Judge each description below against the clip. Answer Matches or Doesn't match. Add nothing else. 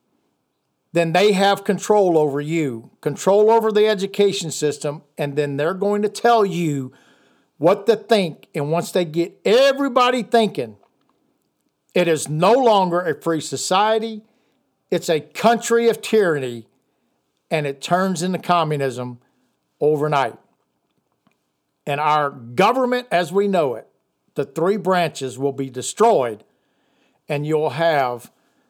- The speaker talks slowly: Matches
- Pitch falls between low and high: Matches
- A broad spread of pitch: Matches